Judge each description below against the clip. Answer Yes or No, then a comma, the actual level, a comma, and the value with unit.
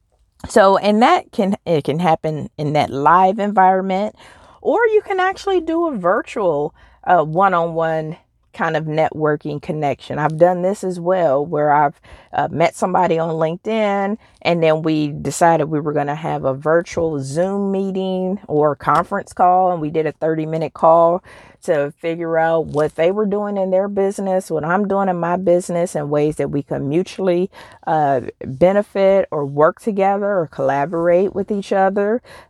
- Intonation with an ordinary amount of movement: Yes, average, 4.2 semitones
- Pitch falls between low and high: Yes, medium, 170 Hz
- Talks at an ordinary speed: Yes, average, 170 wpm